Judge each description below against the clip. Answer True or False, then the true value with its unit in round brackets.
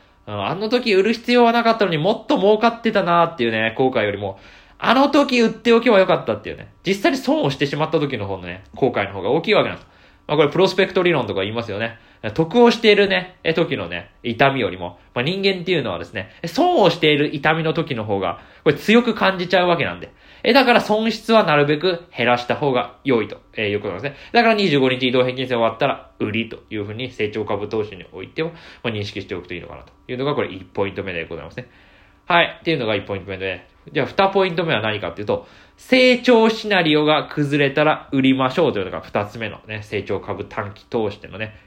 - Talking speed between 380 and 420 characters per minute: False (460 characters per minute)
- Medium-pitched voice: True (145 Hz)